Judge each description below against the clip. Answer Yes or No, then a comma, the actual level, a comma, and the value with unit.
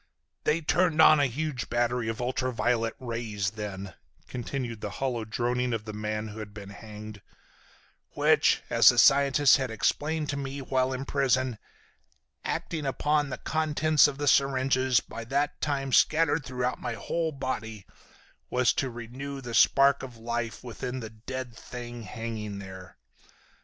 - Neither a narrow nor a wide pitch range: Yes, average, 3.6 semitones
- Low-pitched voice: Yes, low, 125 Hz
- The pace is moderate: Yes, average, 155 wpm